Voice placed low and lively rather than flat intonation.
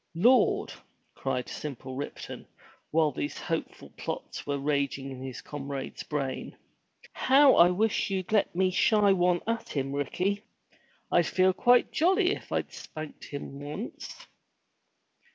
No: medium, 165 Hz; wide, 6.4 semitones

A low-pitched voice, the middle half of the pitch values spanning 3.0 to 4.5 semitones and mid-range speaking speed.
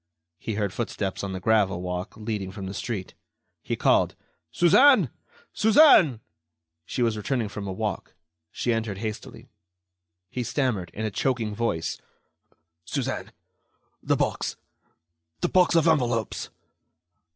No: low, 110 Hz; average, 4.2 semitones; slow, 130 wpm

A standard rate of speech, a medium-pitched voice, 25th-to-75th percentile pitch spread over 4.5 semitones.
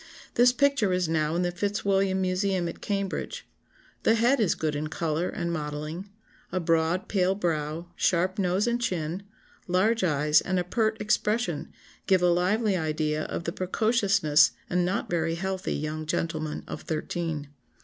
No: average, 160 wpm; medium, 180 Hz; average, 3.7 semitones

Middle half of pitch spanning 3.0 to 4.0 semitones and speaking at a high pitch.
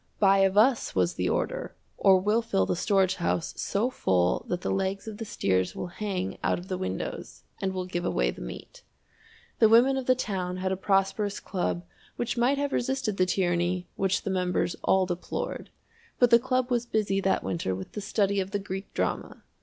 Yes: average, 3.4 semitones; high, 195 Hz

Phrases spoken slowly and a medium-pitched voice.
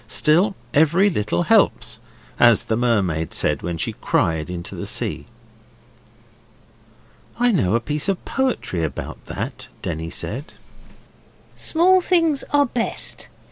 No: slow, 125 wpm; low, 130 Hz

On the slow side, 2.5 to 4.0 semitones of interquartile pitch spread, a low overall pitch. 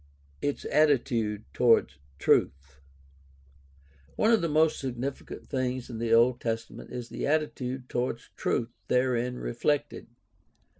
Yes: slow, 120 wpm; average, 3.4 semitones; low, 125 Hz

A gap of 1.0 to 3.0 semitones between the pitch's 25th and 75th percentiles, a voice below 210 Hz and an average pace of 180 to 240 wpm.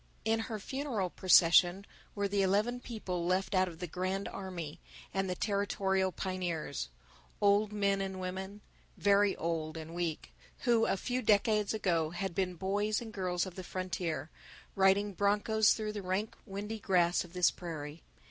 No: narrow, 2.5 semitones; high, 190 Hz; average, 160 wpm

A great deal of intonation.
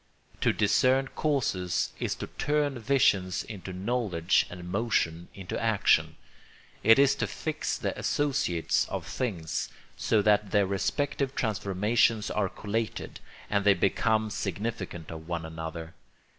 No: average, 4.9 semitones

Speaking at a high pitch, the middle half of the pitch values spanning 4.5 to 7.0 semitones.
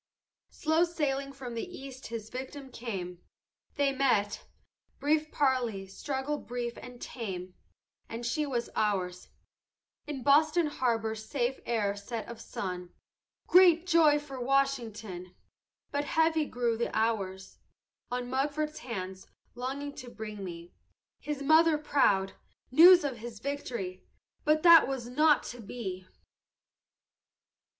Yes: very high, 250 Hz; average, 5.1 semitones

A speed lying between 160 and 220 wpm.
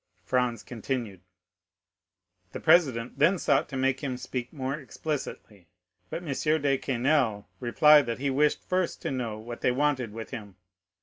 No: average, 150 wpm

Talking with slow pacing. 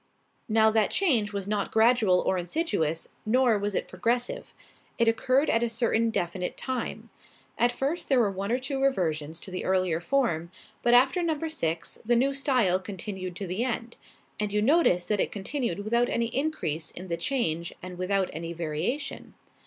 No: average, 175 wpm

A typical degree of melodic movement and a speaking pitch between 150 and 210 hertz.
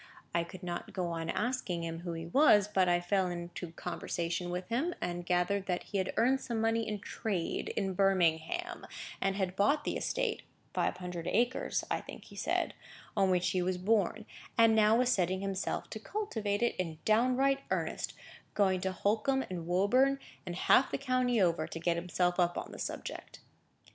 Yes: average, 4.4 semitones; high, 190 Hz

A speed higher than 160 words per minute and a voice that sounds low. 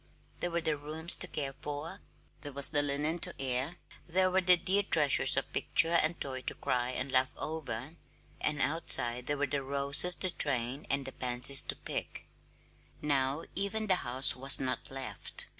No: average, 180 wpm; medium, 145 Hz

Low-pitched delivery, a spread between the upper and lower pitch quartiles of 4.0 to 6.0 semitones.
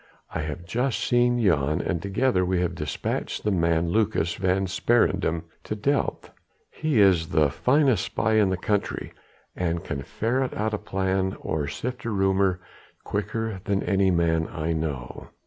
Yes: very low, 95 Hz; average, 4.5 semitones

